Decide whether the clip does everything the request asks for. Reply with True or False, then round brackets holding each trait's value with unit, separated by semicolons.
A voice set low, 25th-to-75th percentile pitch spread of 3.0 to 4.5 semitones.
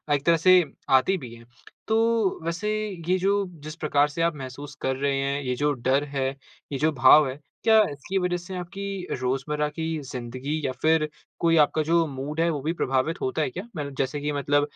False (150 Hz; 3.7 semitones)